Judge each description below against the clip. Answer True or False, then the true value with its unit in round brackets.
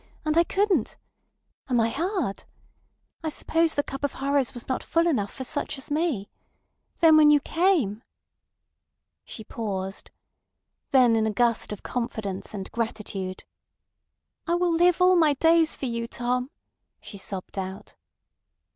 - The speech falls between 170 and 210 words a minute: False (150 wpm)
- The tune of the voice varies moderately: False (7.0 semitones)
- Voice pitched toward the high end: True (260 Hz)